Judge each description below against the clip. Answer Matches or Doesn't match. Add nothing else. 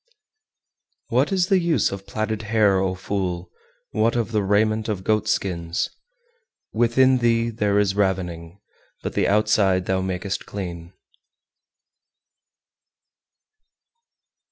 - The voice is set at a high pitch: Doesn't match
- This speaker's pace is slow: Matches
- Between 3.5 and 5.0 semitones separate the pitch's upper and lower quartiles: Doesn't match